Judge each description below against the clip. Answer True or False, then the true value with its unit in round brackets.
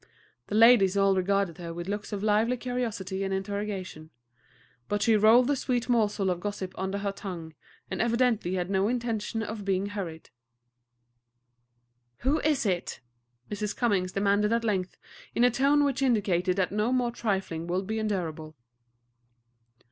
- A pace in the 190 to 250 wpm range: False (155 wpm)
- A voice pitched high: True (205 Hz)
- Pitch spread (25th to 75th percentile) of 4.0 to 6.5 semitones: False (3.5 semitones)